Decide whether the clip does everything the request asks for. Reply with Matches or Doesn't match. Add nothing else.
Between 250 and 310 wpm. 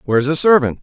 Doesn't match